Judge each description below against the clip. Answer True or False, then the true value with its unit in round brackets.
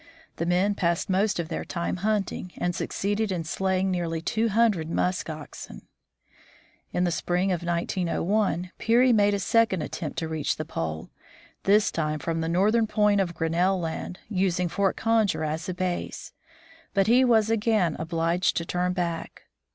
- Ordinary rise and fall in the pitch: True (3.5 semitones)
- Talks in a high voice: False (180 Hz)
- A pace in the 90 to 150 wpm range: False (165 wpm)